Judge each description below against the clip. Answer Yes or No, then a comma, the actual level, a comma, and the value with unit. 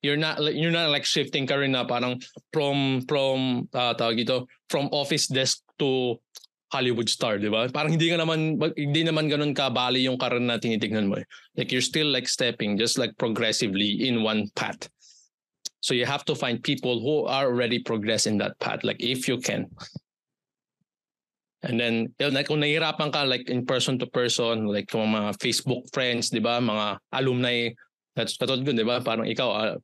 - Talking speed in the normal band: No, fast, 185 wpm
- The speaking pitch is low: Yes, low, 125 Hz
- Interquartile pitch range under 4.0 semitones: Yes, average, 3.6 semitones